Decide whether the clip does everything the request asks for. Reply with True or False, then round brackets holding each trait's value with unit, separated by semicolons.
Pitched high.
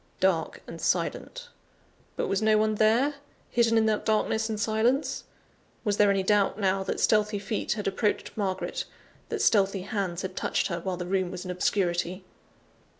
True (205 Hz)